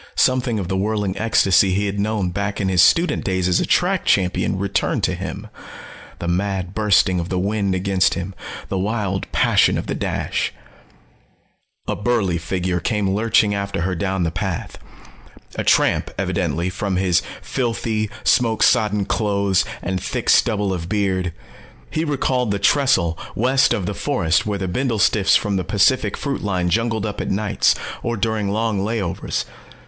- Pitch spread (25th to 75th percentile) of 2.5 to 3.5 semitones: Yes, average, 2.8 semitones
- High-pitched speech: No, low, 100 Hz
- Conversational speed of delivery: Yes, average, 165 wpm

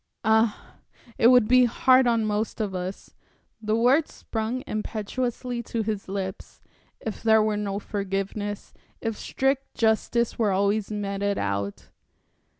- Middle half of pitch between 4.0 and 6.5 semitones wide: No, average, 2.7 semitones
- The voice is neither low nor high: No, high, 215 Hz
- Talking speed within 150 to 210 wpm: No, slow, 135 wpm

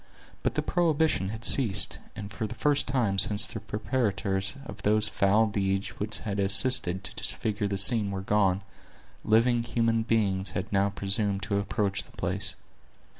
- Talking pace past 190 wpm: No, average, 165 wpm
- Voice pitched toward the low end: Yes, low, 105 Hz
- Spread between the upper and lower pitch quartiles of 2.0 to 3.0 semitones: Yes, narrow, 2.6 semitones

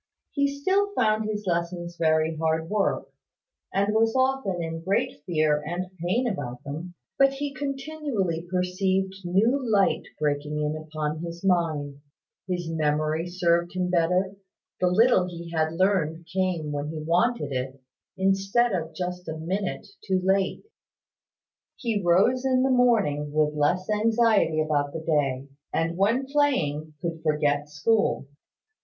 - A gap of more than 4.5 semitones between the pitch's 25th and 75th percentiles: Yes, average, 5.0 semitones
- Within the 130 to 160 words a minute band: Yes, average, 140 wpm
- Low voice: No, medium, 180 Hz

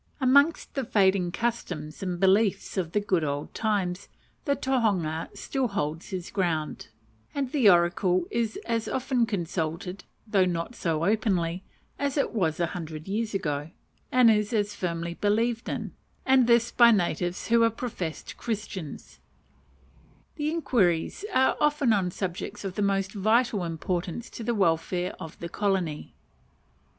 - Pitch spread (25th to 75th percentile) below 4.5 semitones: No, average, 5.1 semitones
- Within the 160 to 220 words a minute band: No, average, 145 wpm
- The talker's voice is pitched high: Yes, high, 195 Hz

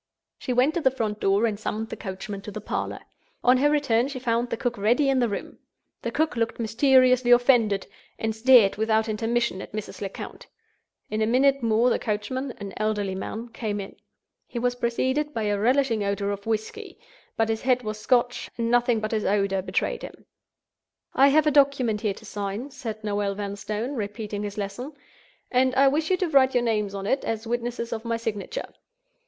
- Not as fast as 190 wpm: No, average, 195 wpm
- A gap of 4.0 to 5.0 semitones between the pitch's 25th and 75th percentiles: No, average, 3.4 semitones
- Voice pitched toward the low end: No, high, 230 Hz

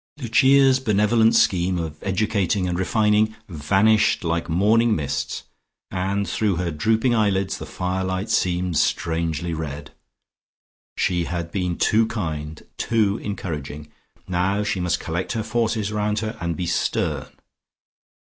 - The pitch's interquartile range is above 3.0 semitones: Yes, average, 4.2 semitones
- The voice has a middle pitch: No, very low, 95 Hz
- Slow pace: Yes, slow, 130 wpm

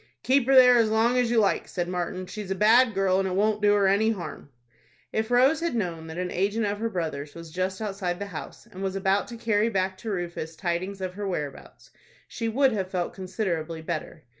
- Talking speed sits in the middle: No, fast, 225 wpm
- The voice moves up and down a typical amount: Yes, average, 3.6 semitones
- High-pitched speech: Yes, high, 195 Hz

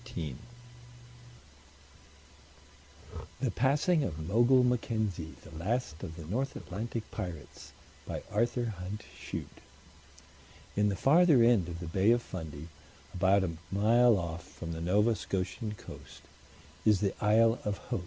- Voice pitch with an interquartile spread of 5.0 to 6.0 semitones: Yes, wide, 5.4 semitones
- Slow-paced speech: Yes, slow, 125 wpm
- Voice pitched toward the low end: Yes, low, 105 Hz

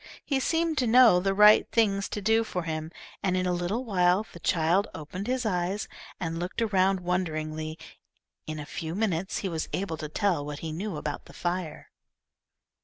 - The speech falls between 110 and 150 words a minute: No, average, 185 wpm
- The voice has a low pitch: No, medium, 180 Hz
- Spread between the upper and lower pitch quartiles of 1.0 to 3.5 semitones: No, average, 4.4 semitones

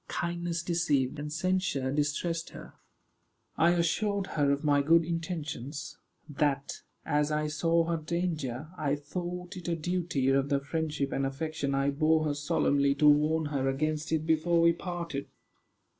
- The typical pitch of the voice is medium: Yes, medium, 155 Hz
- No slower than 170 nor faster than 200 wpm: No, average, 155 wpm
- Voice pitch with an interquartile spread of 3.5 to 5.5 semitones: No, average, 2.9 semitones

